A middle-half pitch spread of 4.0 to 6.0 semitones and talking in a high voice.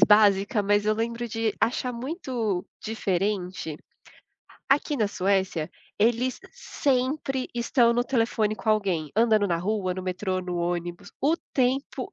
Yes: average, 4.3 semitones; high, 215 Hz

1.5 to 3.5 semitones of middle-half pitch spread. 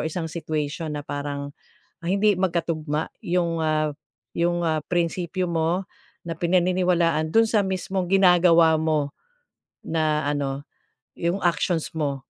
Yes: narrow, 2.6 semitones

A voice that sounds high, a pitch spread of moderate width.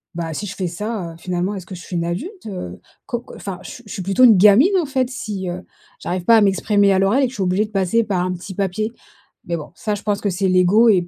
Yes: high, 195 Hz; average, 3.2 semitones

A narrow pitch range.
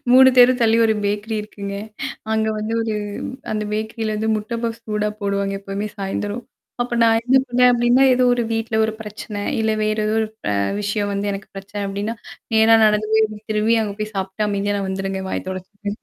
Yes: narrow, 1.8 semitones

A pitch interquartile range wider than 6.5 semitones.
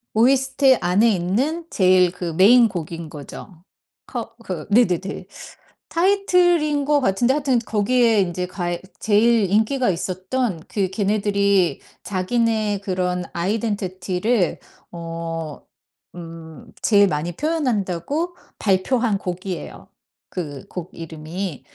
No: average, 5.2 semitones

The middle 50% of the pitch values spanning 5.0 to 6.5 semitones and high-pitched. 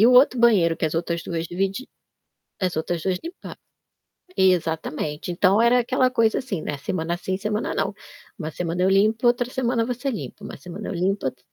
Yes: wide, 5.6 semitones; high, 195 Hz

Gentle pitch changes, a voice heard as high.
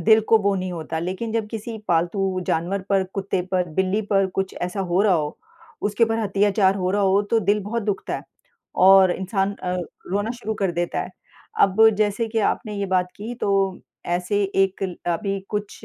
Yes: narrow, 2.1 semitones; high, 195 Hz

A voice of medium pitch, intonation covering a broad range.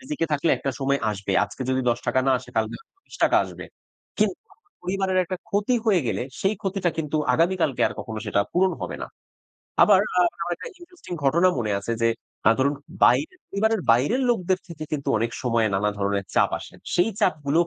Yes: medium, 160 Hz; wide, 8.1 semitones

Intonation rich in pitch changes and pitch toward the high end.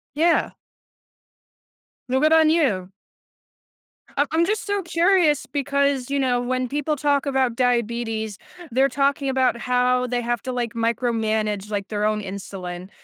No: average, 4.1 semitones; very high, 250 Hz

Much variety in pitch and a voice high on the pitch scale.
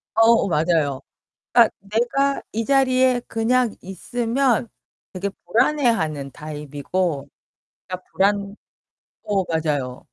Yes: wide, 7.2 semitones; high, 200 Hz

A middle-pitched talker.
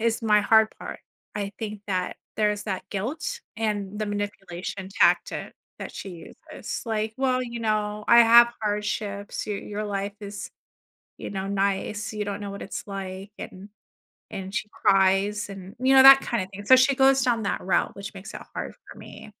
No: high, 210 Hz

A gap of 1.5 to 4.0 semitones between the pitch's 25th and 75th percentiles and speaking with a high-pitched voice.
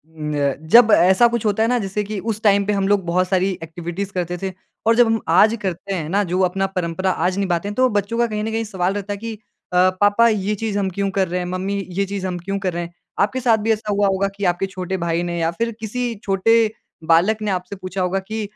Yes: average, 2.8 semitones; high, 195 Hz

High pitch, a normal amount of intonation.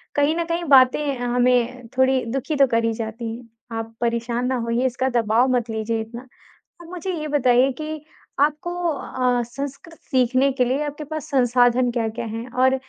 Yes: very high, 250 Hz; average, 3.0 semitones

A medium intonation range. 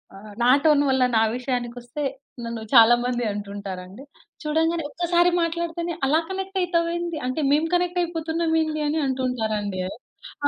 No: wide, 5.9 semitones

